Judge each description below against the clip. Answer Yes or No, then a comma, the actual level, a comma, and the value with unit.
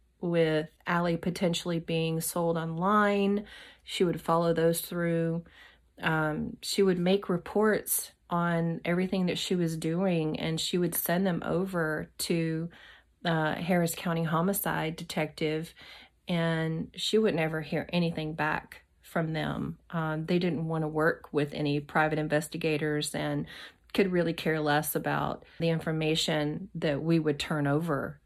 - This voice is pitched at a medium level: Yes, medium, 165 Hz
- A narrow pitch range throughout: Yes, narrow, 2.0 semitones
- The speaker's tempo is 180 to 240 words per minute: No, average, 140 wpm